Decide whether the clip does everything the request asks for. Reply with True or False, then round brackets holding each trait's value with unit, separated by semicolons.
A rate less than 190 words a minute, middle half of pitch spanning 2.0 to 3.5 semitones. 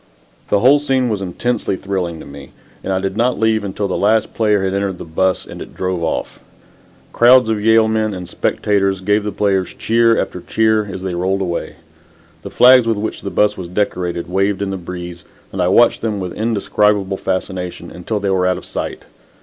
False (205 wpm; 3.0 semitones)